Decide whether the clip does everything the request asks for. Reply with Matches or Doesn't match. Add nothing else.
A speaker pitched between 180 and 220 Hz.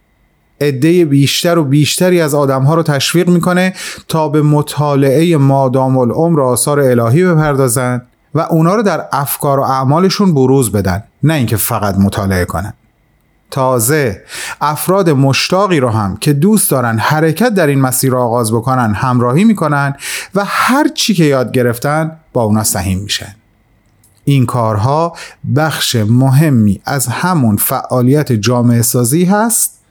Doesn't match